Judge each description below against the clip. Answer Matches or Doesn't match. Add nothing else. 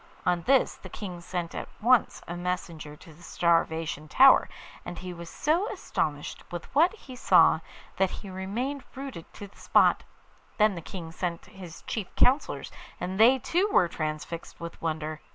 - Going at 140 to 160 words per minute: Doesn't match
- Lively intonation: Matches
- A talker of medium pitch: Matches